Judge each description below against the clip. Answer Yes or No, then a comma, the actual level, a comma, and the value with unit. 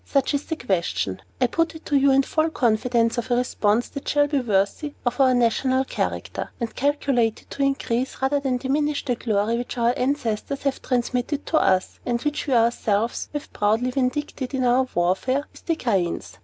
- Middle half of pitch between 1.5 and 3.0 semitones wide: No, average, 3.4 semitones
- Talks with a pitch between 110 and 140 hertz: No, very high, 250 Hz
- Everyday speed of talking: Yes, average, 190 wpm